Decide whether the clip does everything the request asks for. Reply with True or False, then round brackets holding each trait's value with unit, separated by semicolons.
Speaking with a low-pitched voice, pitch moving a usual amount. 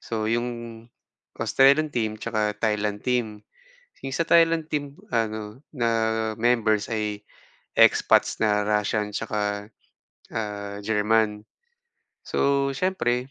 True (110 Hz; 3.0 semitones)